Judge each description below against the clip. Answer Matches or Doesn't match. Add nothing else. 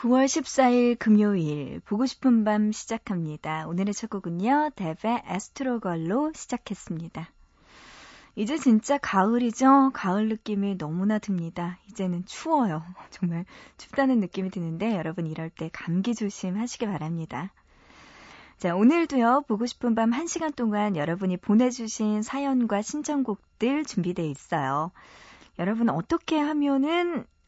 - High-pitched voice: Matches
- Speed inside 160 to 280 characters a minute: Doesn't match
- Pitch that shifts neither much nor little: Doesn't match